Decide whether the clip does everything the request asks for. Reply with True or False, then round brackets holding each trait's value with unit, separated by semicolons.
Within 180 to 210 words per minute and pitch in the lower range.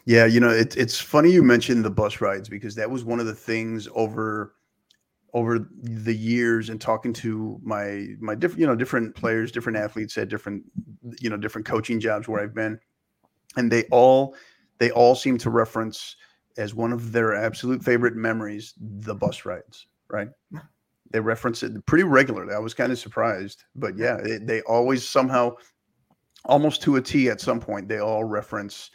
True (185 wpm; 115 Hz)